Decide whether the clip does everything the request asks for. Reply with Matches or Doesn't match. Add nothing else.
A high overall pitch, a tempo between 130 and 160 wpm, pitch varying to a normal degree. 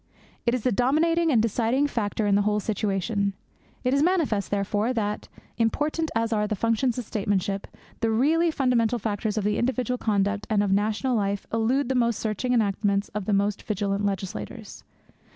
Doesn't match